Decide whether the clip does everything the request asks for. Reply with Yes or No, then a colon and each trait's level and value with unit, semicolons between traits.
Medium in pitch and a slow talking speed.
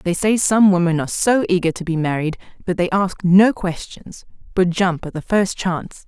No: medium, 180 Hz; fast, 205 wpm